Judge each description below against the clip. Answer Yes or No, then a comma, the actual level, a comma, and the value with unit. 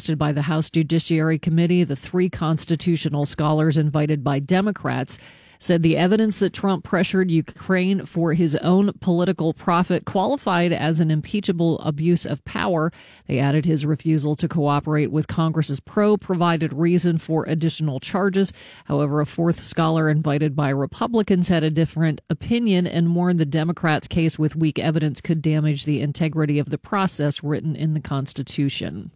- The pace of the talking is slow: No, average, 155 wpm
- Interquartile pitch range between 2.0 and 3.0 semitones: Yes, narrow, 2.5 semitones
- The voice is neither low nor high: Yes, medium, 160 Hz